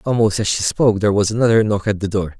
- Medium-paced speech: No, fast, 275 wpm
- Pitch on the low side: Yes, low, 105 Hz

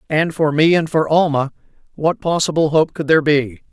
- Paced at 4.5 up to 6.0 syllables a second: Yes, 5.3 syllables/s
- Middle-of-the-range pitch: Yes, medium, 155 Hz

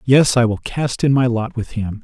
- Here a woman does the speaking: No, male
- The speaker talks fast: Yes, fast, 265 wpm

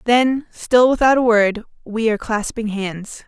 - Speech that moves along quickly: No, average, 165 wpm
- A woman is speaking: Yes, female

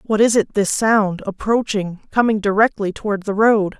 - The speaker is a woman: Yes, female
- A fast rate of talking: No, average, 175 wpm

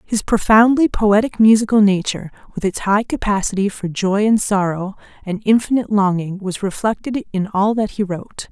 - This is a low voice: No, high, 205 Hz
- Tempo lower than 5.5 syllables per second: Yes, 5.2 syllables/s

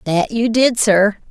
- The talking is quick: No, average, 185 wpm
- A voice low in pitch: No, high, 215 Hz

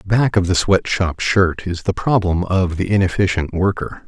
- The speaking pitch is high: No, very low, 95 Hz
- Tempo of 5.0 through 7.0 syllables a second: No, 4.6 syllables/s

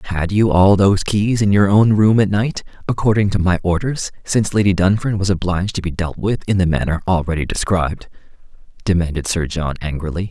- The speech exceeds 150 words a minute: Yes, average, 190 wpm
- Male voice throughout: Yes, male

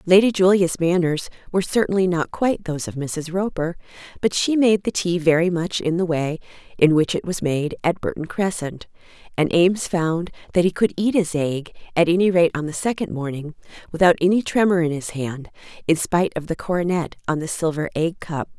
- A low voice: No, medium, 170 Hz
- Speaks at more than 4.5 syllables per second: Yes, 5.5 syllables/s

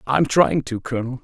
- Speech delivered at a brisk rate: No, average, 195 wpm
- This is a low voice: Yes, low, 130 Hz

